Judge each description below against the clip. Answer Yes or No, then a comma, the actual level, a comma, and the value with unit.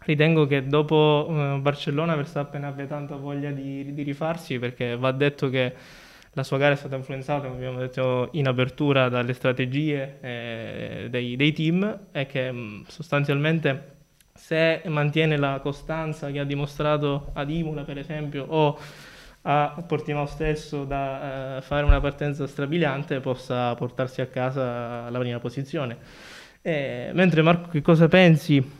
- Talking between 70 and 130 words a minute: No, average, 145 wpm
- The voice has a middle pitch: Yes, medium, 145 Hz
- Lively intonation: No, narrow, 2.4 semitones